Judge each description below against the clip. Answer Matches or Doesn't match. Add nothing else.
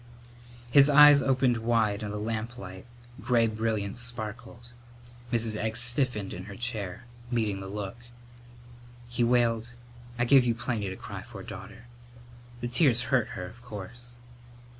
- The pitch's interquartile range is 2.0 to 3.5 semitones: Matches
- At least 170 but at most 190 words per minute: Doesn't match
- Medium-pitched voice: Doesn't match